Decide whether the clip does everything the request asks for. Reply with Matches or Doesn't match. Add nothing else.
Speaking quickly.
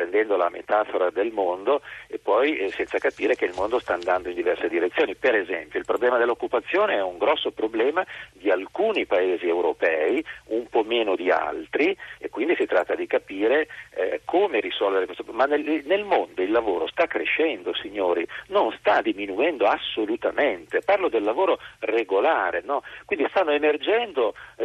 Doesn't match